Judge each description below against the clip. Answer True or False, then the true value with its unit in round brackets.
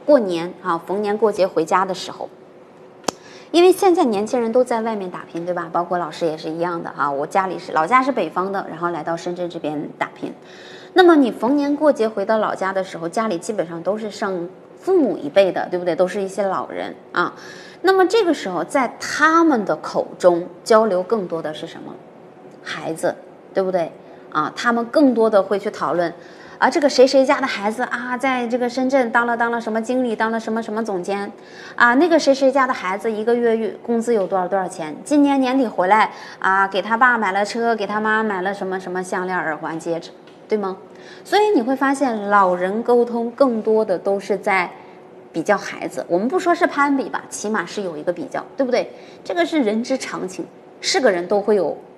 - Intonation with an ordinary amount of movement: False (5.9 semitones)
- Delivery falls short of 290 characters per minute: False (300 characters per minute)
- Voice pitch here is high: True (215 Hz)